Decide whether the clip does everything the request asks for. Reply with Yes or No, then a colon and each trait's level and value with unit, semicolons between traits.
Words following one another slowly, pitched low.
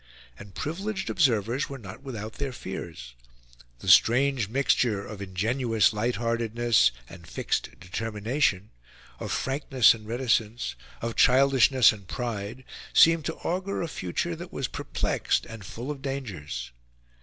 Yes: slow, 130 wpm; low, 120 Hz